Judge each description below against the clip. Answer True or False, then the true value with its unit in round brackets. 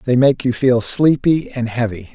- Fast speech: False (195 wpm)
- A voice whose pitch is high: False (125 Hz)